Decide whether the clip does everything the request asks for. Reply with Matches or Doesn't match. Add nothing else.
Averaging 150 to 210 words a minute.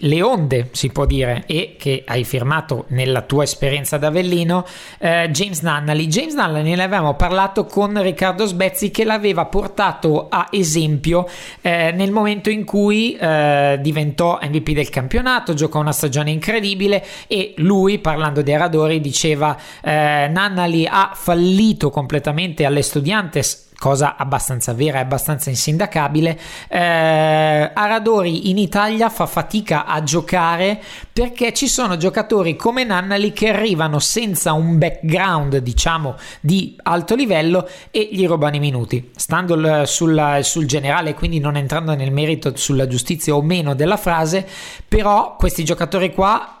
Doesn't match